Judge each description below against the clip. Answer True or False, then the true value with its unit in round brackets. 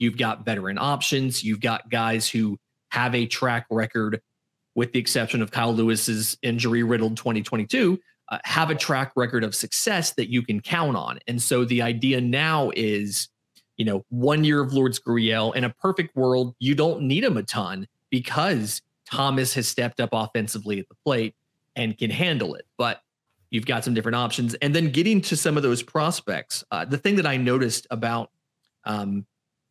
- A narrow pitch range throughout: False (3.8 semitones)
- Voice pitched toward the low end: True (120 Hz)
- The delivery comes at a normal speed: True (185 wpm)